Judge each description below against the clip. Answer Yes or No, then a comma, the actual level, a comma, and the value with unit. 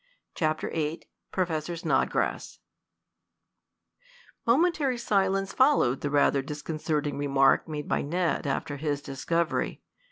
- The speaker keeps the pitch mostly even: No, average, 4.7 semitones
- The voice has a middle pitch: Yes, medium, 155 Hz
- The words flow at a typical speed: No, slow, 100 wpm